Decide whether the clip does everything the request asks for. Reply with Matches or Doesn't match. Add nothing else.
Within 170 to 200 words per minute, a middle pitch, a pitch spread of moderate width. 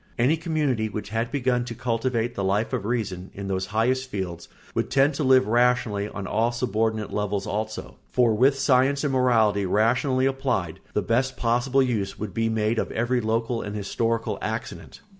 Doesn't match